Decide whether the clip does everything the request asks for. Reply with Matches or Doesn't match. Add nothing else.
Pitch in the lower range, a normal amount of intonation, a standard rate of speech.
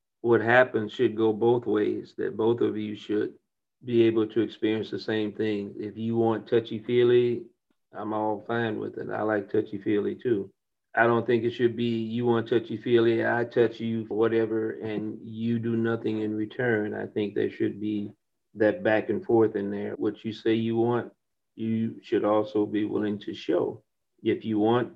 Doesn't match